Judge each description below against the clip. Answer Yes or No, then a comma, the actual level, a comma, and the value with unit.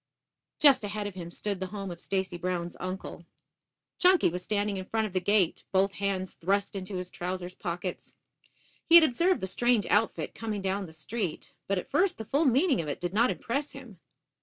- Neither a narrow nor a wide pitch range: Yes, average, 3.7 semitones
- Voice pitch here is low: No, high, 200 Hz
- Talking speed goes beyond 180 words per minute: Yes, average, 200 wpm